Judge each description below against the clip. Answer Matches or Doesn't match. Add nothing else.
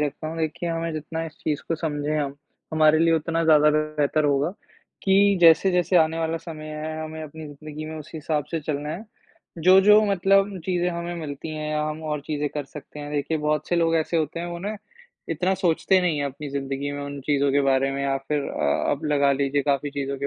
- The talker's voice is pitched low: Doesn't match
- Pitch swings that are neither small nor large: Doesn't match